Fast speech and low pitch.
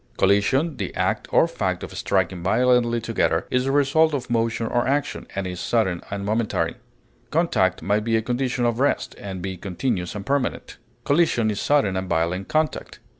No: average, 175 wpm; low, 115 Hz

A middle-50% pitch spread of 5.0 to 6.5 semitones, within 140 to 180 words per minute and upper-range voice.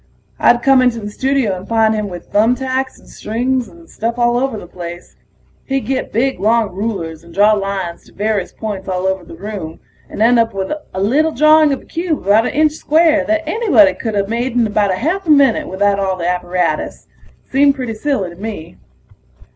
No: wide, 5.6 semitones; fast, 205 wpm; high, 225 Hz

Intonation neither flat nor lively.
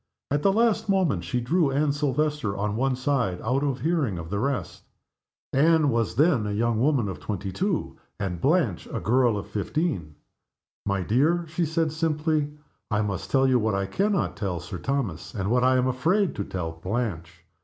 No: wide, 7.2 semitones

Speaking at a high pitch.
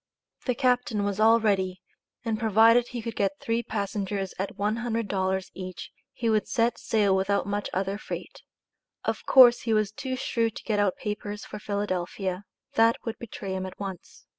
Yes: high, 210 Hz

